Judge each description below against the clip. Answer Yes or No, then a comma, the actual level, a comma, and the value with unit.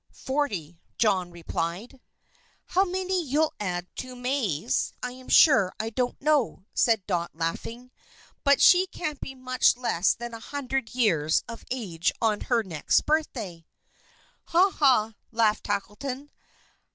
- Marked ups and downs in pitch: Yes, wide, 6.4 semitones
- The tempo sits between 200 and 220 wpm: No, slow, 135 wpm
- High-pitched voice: Yes, high, 235 Hz